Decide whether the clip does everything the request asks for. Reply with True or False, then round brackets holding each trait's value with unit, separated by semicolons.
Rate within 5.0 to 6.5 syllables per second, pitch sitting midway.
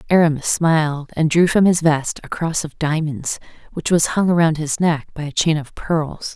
False (4.8 syllables/s; 160 Hz)